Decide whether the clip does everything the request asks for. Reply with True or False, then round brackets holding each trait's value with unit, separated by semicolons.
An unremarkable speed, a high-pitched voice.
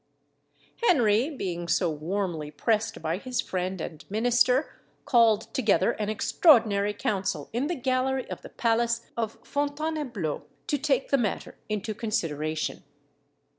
False (130 wpm; 220 Hz)